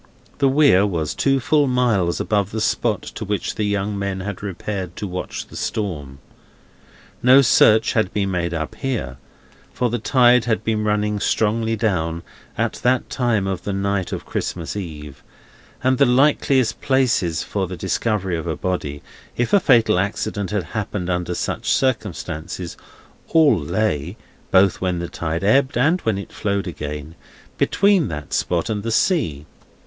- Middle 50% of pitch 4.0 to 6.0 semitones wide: Yes, average, 5.1 semitones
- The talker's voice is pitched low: Yes, low, 100 Hz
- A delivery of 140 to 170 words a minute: Yes, average, 160 wpm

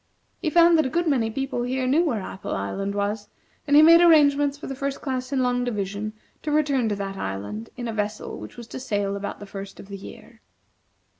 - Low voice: No, high, 245 Hz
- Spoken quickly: Yes, fast, 225 wpm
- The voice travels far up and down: Yes, wide, 5.9 semitones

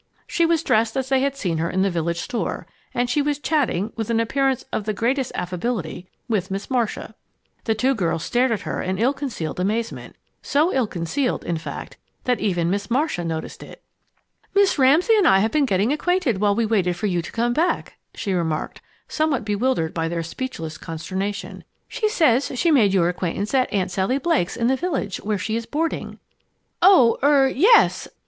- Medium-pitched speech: No, high, 230 Hz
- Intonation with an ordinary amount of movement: No, wide, 6.5 semitones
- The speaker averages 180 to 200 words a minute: Yes, average, 195 wpm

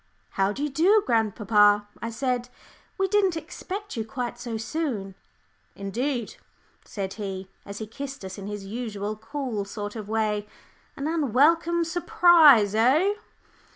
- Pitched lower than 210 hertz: No, high, 235 Hz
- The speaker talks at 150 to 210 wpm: No, average, 140 wpm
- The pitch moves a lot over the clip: Yes, wide, 7.0 semitones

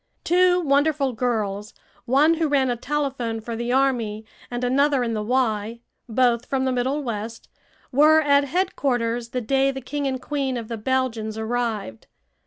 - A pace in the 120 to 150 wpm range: No, average, 165 wpm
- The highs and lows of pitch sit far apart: No, average, 3.4 semitones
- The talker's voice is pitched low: No, very high, 255 Hz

